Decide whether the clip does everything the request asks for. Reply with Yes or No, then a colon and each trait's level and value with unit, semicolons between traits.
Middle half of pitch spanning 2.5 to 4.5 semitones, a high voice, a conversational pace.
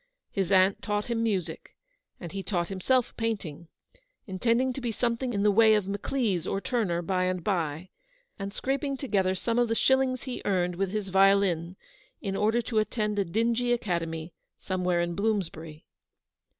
Yes: average, 4.1 semitones; high, 200 Hz; average, 170 wpm